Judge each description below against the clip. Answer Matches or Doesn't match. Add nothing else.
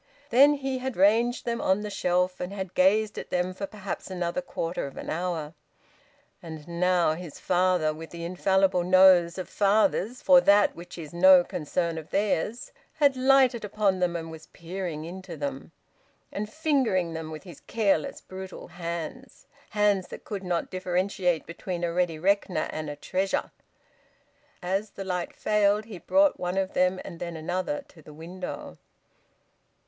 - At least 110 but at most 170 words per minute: Matches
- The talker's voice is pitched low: Doesn't match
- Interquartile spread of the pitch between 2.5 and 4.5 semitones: Matches